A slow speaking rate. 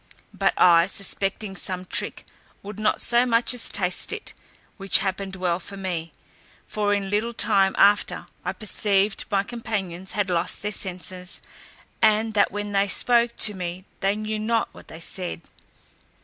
No: average, 160 wpm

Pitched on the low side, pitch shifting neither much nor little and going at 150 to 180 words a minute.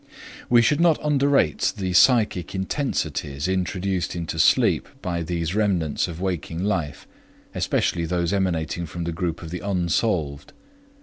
No: very low, 90 Hz; average, 3.3 semitones; slow, 135 wpm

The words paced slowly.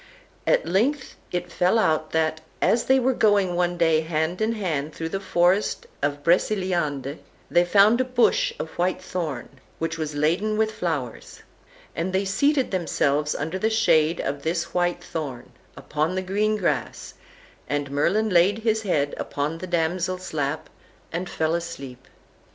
No: average, 155 wpm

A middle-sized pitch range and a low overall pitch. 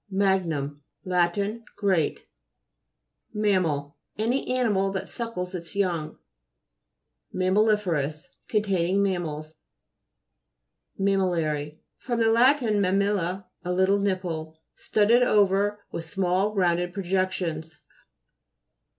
No: average, 3.3 semitones; high, 190 Hz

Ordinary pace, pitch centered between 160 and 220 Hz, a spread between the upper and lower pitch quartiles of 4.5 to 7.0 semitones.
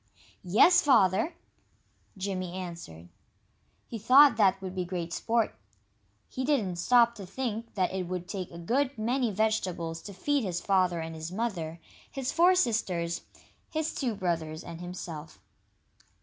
Yes: average, 145 wpm; high, 190 Hz; wide, 5.4 semitones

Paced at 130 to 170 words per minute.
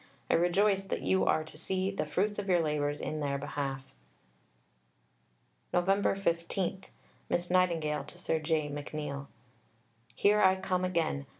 Yes: average, 140 wpm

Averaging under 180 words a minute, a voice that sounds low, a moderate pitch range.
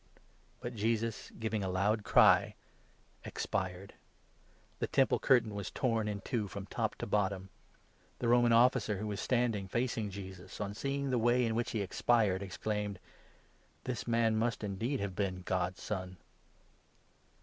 Yes: average, 160 wpm; low, 105 Hz; average, 3.2 semitones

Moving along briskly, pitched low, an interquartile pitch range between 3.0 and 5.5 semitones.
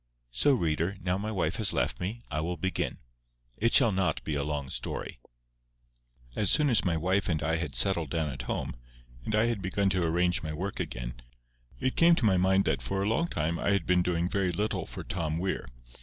Yes: fast, 215 wpm; very low, 90 Hz; average, 3.7 semitones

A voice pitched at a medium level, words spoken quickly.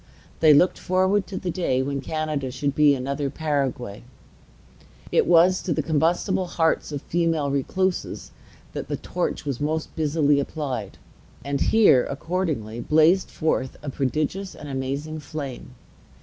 No: medium, 150 Hz; average, 140 wpm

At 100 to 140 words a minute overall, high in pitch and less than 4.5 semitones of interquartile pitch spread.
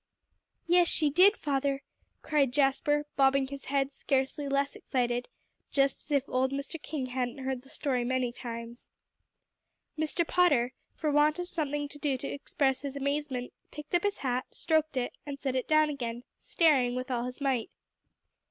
No: average, 170 wpm; very high, 275 Hz; narrow, 2.6 semitones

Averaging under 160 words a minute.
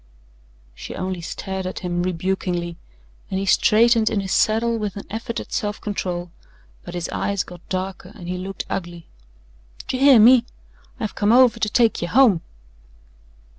No: average, 165 wpm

